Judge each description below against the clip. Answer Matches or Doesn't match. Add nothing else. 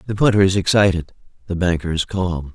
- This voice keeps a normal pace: Matches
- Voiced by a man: Matches